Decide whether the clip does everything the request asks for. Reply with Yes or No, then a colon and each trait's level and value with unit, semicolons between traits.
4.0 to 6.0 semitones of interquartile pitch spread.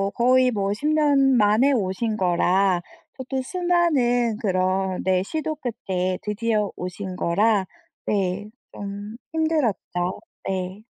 Yes: wide, 5.4 semitones